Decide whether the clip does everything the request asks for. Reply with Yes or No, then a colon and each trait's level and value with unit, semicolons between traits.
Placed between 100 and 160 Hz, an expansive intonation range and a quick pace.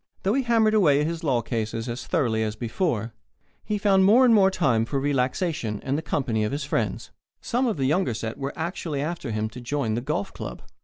Yes: medium, 140 Hz; wide, 8.0 semitones; fast, 210 wpm